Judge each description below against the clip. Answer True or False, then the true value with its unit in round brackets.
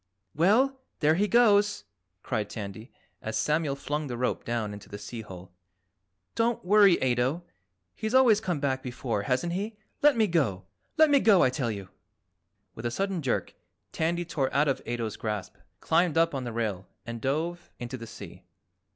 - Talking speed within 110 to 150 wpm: False (175 wpm)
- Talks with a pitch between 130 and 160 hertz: True (140 Hz)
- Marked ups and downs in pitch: True (8.1 semitones)